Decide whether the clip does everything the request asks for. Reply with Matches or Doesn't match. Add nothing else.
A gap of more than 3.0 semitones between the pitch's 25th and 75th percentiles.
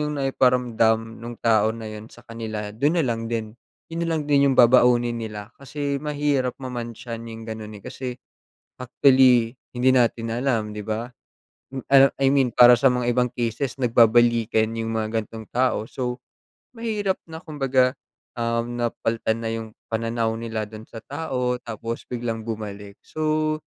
Doesn't match